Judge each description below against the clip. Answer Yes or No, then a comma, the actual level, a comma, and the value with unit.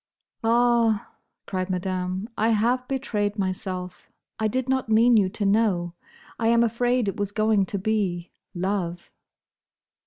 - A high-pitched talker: Yes, high, 210 Hz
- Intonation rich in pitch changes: No, average, 3.6 semitones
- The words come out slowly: Yes, slow, 130 wpm